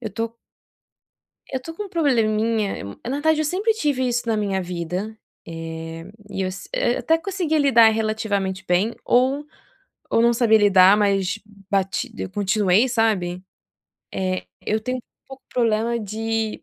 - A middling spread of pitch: Yes, average, 4.7 semitones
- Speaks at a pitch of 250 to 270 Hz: No, high, 220 Hz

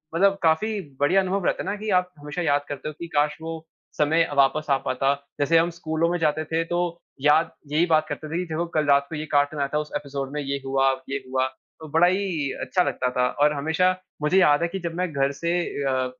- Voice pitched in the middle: Yes, medium, 155 Hz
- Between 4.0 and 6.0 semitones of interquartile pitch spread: No, average, 3.0 semitones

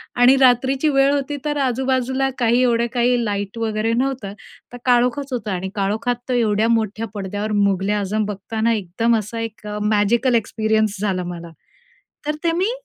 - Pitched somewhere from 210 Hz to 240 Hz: Yes, high, 230 Hz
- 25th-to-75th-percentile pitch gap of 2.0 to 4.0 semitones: Yes, average, 3.2 semitones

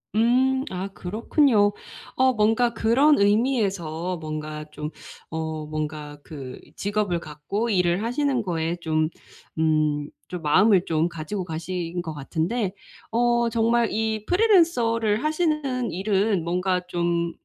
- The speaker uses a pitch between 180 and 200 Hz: Yes, high, 190 Hz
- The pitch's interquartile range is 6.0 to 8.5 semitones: Yes, wide, 6.3 semitones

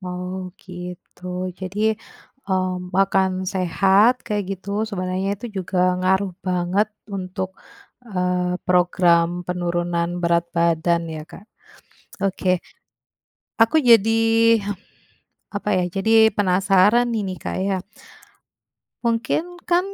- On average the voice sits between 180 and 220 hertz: Yes, medium, 185 Hz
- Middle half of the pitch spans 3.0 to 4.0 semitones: No, narrow, 2.5 semitones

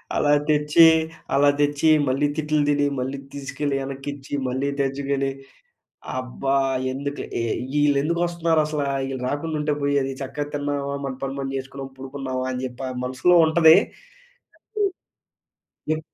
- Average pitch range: No, narrow, 1.7 semitones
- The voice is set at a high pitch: No, medium, 140 Hz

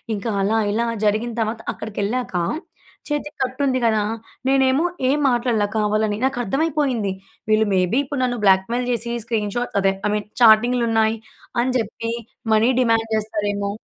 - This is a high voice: Yes, high, 230 Hz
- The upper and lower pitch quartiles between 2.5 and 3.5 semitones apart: Yes, average, 2.9 semitones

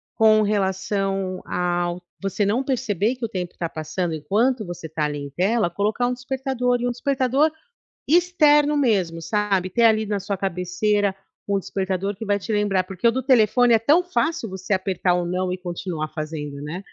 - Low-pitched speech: No, high, 200 Hz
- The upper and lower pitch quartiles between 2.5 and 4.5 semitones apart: No, average, 5.0 semitones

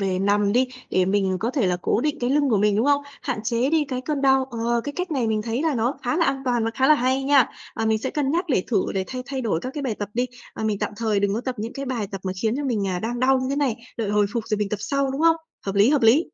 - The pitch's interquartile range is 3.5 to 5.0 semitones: Yes, average, 4.3 semitones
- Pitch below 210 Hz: No, high, 240 Hz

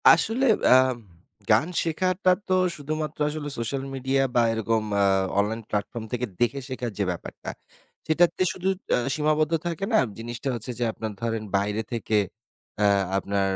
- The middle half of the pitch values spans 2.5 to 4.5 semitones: No, wide, 5.6 semitones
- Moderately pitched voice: No, low, 125 Hz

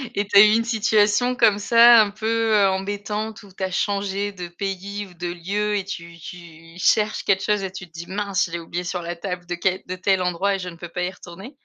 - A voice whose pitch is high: Yes, high, 195 Hz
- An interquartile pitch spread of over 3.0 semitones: No, average, 2.7 semitones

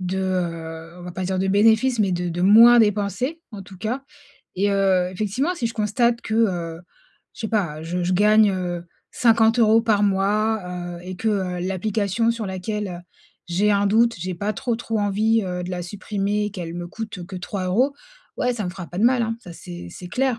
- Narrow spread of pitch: No, average, 3.6 semitones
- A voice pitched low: No, high, 200 Hz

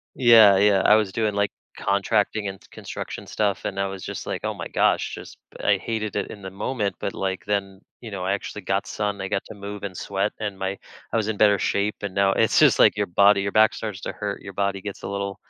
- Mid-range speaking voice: No, low, 100 Hz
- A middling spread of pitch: No, narrow, 1.2 semitones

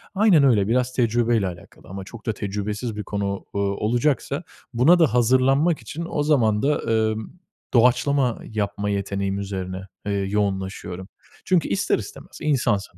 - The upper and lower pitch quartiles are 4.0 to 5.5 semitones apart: Yes, average, 4.6 semitones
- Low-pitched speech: Yes, low, 110 Hz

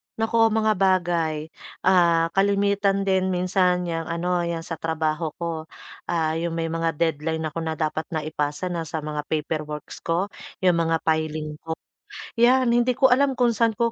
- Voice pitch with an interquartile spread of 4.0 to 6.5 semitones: No, average, 3.5 semitones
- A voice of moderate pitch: Yes, medium, 170 Hz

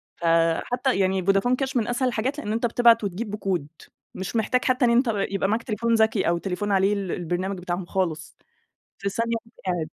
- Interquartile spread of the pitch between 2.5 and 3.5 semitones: No, average, 4.1 semitones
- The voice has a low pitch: No, high, 205 Hz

